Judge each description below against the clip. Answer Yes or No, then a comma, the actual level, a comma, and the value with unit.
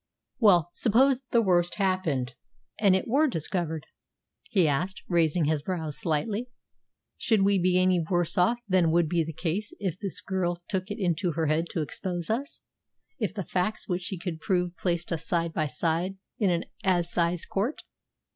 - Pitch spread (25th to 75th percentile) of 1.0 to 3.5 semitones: Yes, average, 2.8 semitones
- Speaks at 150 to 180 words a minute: Yes, average, 175 wpm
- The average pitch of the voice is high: No, medium, 180 Hz